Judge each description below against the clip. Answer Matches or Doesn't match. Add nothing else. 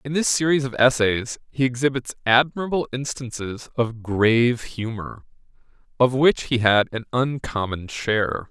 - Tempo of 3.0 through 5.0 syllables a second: Matches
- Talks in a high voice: Doesn't match